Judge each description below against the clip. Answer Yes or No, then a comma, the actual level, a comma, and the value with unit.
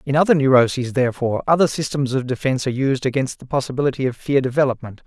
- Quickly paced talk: No, average, 190 wpm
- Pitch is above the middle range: No, low, 135 Hz